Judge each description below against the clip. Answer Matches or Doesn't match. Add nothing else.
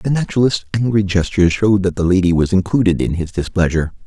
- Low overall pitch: Matches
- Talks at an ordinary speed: Matches